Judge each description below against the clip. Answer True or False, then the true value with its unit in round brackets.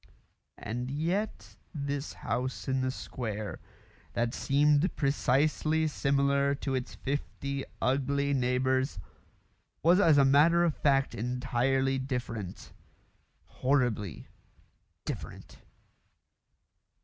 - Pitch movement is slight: True (2.2 semitones)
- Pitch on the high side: False (135 Hz)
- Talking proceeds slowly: True (90 wpm)